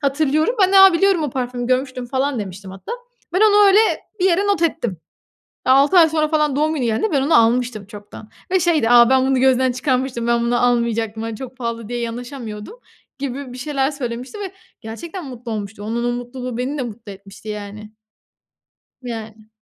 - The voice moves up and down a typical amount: Yes, average, 4.5 semitones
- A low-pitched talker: No, very high, 250 Hz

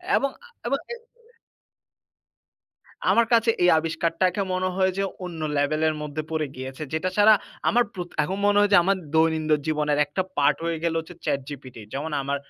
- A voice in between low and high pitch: Yes, medium, 160 Hz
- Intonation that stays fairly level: No, average, 4.1 semitones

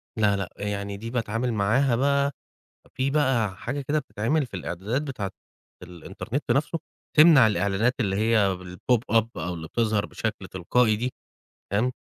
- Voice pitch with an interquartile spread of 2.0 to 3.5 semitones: No, average, 4.6 semitones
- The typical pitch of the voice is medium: No, low, 115 Hz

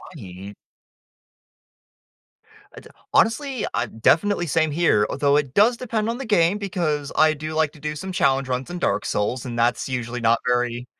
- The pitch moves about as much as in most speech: No, wide, 7.2 semitones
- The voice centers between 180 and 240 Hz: No, medium, 150 Hz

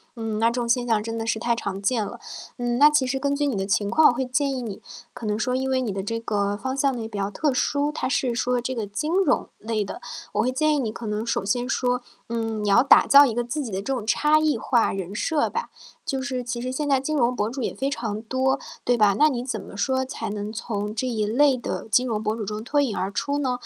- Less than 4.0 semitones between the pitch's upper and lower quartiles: Yes, average, 3.6 semitones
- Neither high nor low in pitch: No, high, 240 Hz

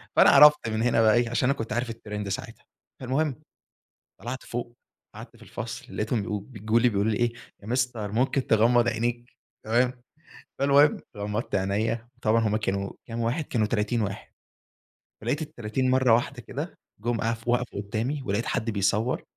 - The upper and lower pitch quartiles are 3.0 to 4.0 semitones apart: No, narrow, 2.4 semitones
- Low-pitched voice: Yes, low, 115 Hz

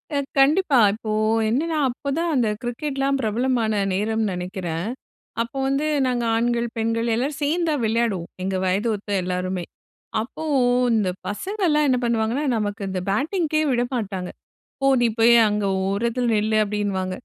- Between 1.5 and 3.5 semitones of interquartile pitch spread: No, average, 4.8 semitones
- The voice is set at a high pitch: Yes, high, 230 Hz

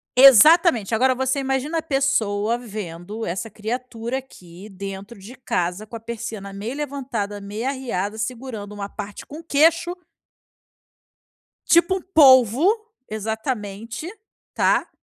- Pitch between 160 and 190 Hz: No, high, 230 Hz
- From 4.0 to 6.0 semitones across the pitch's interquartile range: Yes, average, 4.7 semitones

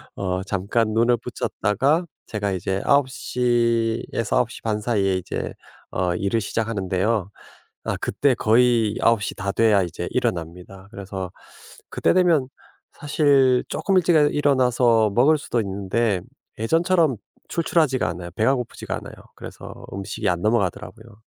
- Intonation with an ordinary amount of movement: Yes, average, 4.5 semitones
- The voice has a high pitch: No, low, 115 Hz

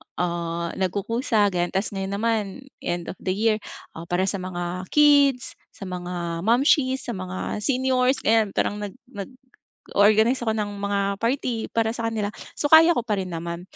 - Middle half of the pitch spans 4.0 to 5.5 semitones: Yes, average, 4.6 semitones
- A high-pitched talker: Yes, high, 205 Hz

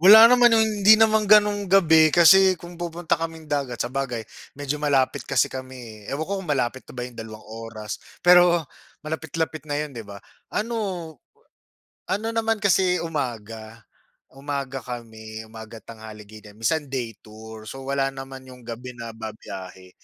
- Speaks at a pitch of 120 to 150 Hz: Yes, low, 135 Hz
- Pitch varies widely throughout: Yes, wide, 7.0 semitones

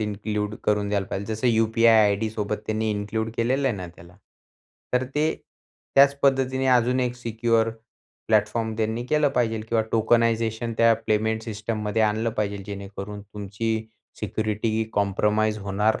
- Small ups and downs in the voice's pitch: Yes, narrow, 1.8 semitones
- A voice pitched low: Yes, low, 110 Hz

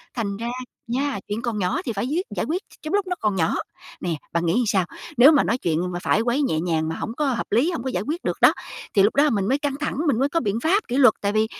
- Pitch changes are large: Yes, wide, 6.3 semitones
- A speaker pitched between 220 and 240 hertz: Yes, high, 235 Hz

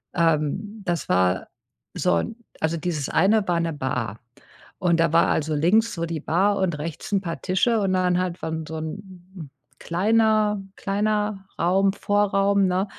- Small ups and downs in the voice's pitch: No, average, 3.6 semitones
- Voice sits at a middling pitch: Yes, medium, 180 Hz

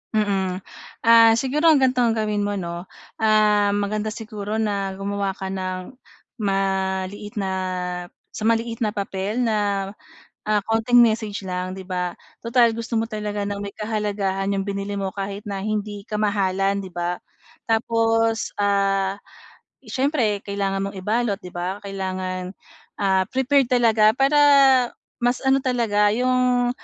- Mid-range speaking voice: No, high, 205 Hz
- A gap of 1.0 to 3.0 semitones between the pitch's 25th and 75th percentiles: Yes, narrow, 2.6 semitones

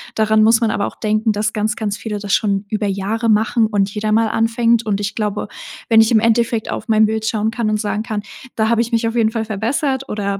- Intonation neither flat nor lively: No, narrow, 1.4 semitones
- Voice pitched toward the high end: Yes, high, 220 Hz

